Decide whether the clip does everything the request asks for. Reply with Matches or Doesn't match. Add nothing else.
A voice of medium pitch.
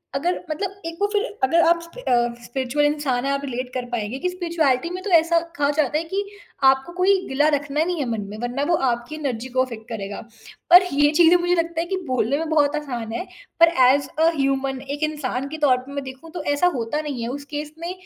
Doesn't match